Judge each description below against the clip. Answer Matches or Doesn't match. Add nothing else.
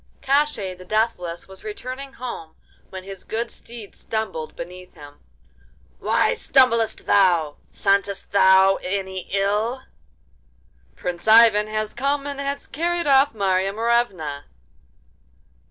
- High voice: Matches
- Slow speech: Matches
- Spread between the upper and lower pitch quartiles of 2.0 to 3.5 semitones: Doesn't match